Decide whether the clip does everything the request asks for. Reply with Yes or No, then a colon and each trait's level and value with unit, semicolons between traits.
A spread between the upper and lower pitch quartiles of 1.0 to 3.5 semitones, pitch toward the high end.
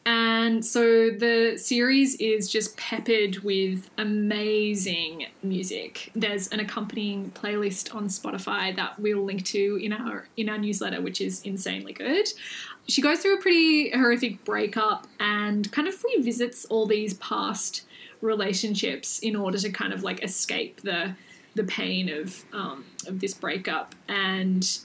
Yes: average, 2.9 semitones; high, 210 Hz